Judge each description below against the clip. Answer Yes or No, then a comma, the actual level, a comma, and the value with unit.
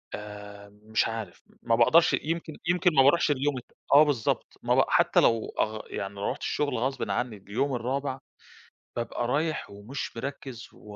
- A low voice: Yes, low, 125 Hz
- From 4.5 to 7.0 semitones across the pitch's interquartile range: Yes, average, 4.8 semitones